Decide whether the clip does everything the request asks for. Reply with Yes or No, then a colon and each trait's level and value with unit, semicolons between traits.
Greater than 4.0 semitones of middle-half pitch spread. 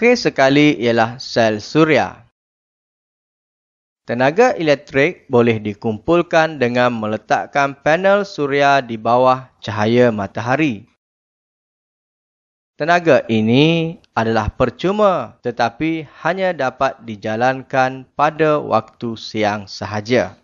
Yes: average, 5.3 semitones